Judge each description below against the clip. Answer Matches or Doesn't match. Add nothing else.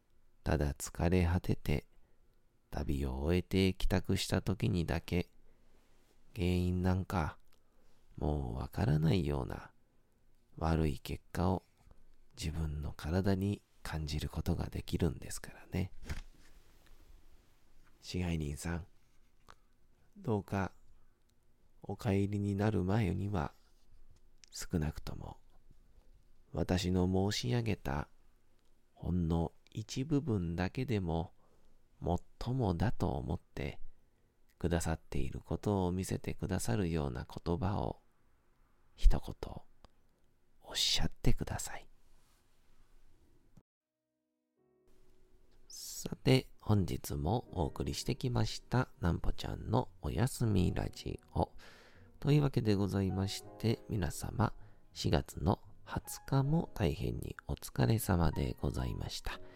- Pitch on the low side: Matches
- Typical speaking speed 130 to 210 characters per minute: Matches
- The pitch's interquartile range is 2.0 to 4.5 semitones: Doesn't match